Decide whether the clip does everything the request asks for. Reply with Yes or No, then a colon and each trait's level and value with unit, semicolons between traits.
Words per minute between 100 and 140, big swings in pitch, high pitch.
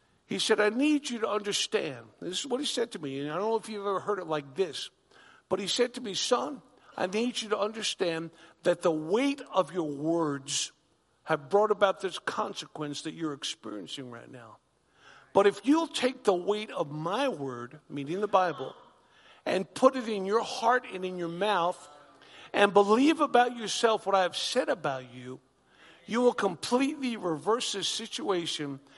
No: average, 185 wpm; wide, 6.5 semitones; high, 205 Hz